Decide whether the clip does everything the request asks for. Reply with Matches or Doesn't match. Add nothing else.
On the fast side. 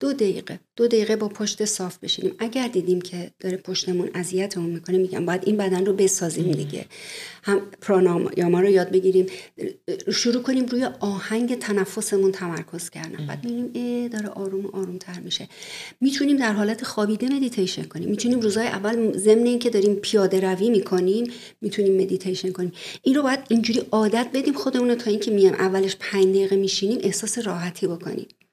Matches